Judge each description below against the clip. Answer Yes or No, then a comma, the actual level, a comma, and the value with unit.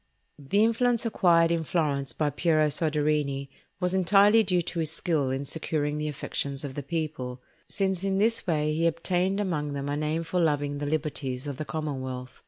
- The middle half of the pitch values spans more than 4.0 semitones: No, average, 3.7 semitones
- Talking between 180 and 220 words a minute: Yes, average, 185 wpm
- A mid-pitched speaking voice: Yes, medium, 155 Hz